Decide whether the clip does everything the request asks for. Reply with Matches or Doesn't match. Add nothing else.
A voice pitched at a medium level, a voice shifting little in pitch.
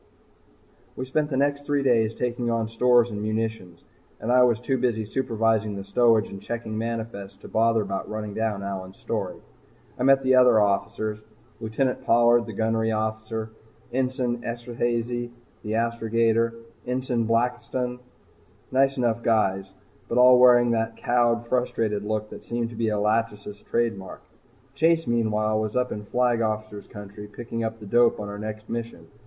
Doesn't match